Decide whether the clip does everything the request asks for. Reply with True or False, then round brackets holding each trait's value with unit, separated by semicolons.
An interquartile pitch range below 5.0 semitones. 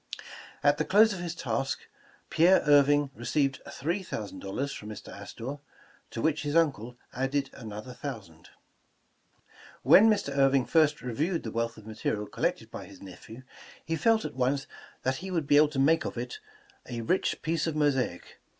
False (5.3 semitones)